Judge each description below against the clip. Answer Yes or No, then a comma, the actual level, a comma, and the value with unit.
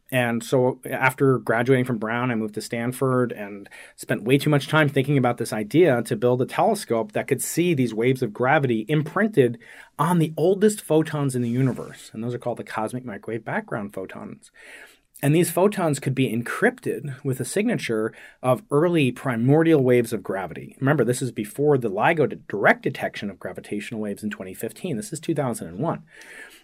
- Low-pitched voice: Yes, low, 130 Hz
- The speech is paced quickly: No, average, 180 wpm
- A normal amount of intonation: Yes, average, 4.3 semitones